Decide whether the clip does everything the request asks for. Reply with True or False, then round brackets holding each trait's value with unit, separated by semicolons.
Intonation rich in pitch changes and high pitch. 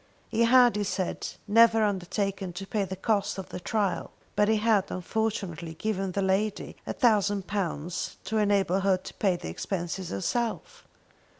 False (2.7 semitones; 200 Hz)